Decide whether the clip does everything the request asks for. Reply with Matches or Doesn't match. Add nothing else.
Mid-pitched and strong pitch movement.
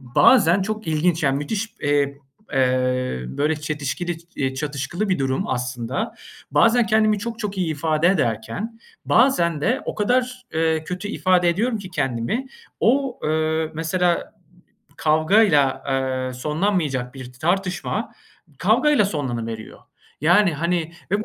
Matches